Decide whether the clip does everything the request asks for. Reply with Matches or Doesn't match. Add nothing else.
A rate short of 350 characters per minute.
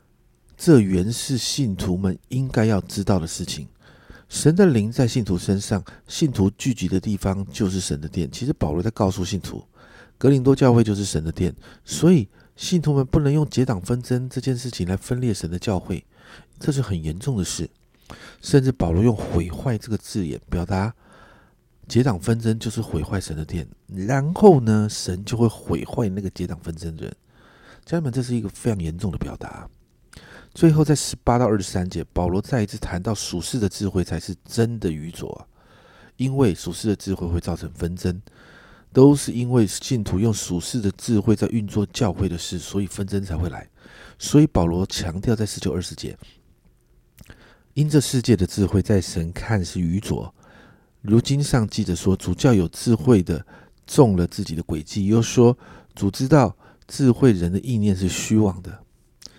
Matches